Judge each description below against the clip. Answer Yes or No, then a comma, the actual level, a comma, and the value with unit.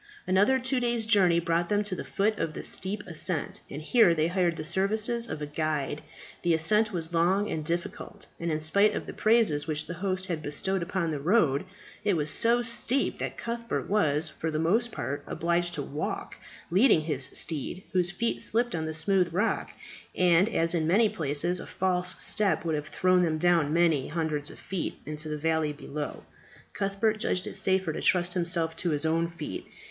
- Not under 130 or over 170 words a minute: No, average, 195 wpm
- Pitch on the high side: No, medium, 175 Hz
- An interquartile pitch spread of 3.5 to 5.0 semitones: Yes, average, 4.1 semitones